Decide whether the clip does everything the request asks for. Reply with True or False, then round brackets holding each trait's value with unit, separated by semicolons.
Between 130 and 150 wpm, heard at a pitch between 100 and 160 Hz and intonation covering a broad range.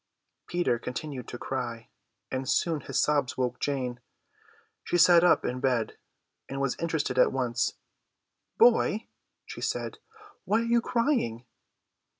True (135 wpm; 135 Hz; 5.8 semitones)